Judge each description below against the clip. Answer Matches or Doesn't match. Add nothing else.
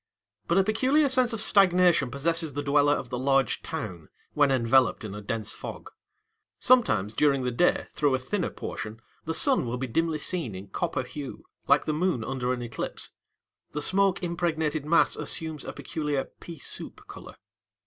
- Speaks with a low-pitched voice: Doesn't match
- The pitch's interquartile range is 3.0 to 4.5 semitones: Doesn't match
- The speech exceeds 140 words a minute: Matches